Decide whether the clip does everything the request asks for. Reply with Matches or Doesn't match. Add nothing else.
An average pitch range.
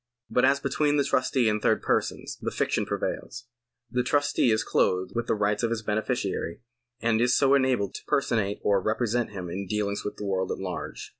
Matches